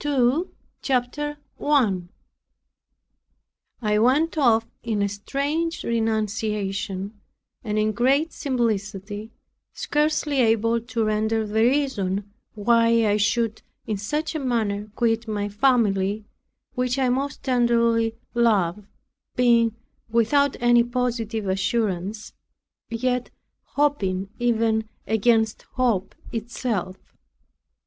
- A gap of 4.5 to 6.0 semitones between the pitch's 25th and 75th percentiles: No, average, 3.0 semitones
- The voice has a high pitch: Yes, high, 230 Hz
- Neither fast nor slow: No, slow, 100 wpm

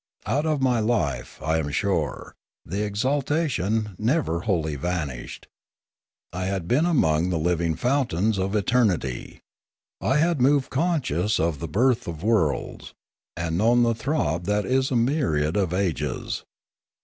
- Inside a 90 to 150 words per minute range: Yes, average, 145 wpm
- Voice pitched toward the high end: No, low, 100 Hz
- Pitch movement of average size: No, wide, 7.5 semitones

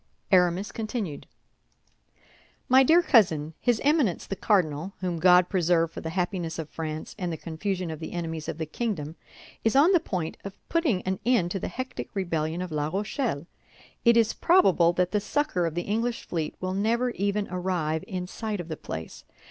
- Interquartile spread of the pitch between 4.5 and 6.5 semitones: Yes, average, 5.1 semitones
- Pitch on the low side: No, medium, 185 Hz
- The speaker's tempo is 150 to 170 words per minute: No, average, 185 wpm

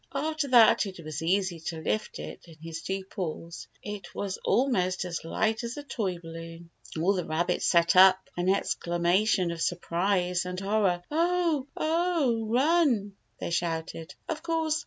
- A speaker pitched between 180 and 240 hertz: Yes, high, 190 Hz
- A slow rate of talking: No, average, 160 wpm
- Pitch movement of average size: No, wide, 5.9 semitones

